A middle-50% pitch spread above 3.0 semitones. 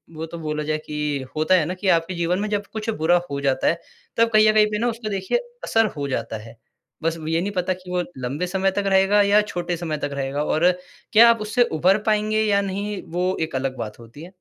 Yes: average, 5.0 semitones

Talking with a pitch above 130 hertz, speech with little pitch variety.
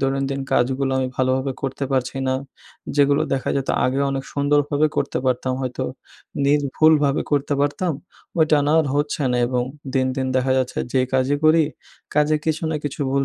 Yes: medium, 140 Hz; narrow, 1.9 semitones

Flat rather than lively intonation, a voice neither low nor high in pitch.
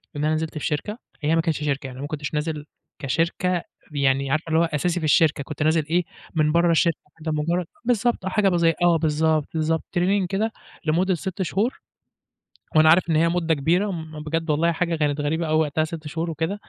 Yes: narrow, 2.2 semitones; medium, 160 Hz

